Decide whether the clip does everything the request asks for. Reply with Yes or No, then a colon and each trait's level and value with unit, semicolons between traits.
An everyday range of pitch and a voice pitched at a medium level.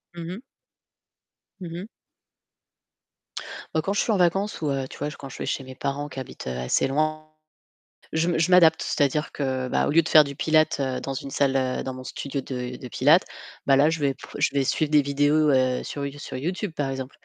Yes: average, 3.0 semitones; medium, 145 Hz